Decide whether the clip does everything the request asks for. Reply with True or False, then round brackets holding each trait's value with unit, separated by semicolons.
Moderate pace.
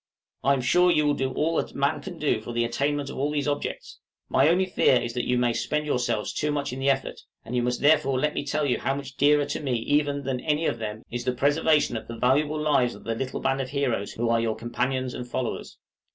False (255 wpm)